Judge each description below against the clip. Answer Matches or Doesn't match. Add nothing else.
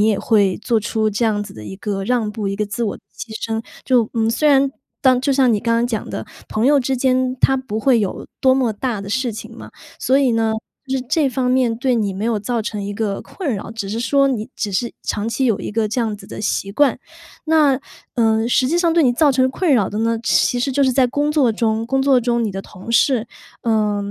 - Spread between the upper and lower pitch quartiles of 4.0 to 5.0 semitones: Doesn't match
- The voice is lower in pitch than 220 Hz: Doesn't match